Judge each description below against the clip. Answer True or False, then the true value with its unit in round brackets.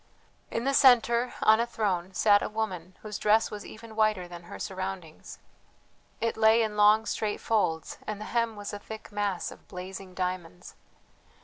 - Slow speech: False (175 wpm)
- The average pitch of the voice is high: True (210 Hz)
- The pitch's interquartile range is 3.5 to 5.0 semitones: False (3.1 semitones)